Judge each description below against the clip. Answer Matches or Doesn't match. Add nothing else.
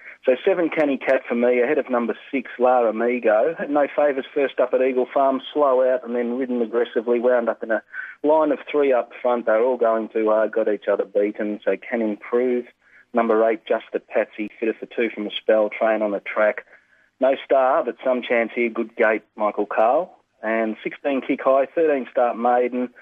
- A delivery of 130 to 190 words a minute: Doesn't match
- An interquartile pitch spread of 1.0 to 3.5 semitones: Matches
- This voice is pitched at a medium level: Doesn't match